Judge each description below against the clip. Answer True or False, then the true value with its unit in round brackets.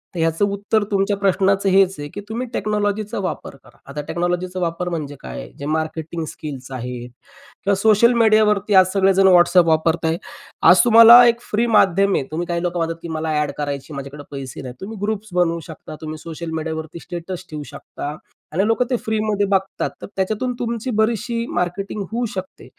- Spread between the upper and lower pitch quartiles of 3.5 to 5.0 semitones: True (4.6 semitones)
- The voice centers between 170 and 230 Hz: True (185 Hz)